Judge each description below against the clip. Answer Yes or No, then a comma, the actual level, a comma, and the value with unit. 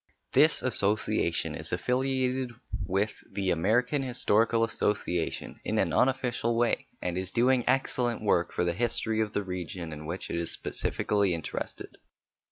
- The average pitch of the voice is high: No, low, 110 Hz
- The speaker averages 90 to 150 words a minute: Yes, average, 145 wpm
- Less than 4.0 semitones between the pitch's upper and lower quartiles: No, wide, 5.4 semitones